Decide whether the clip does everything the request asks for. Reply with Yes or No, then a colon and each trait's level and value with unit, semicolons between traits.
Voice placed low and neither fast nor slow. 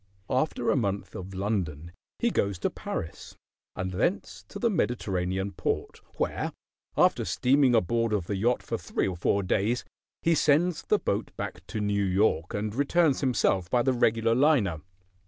Yes: low, 110 Hz; average, 165 wpm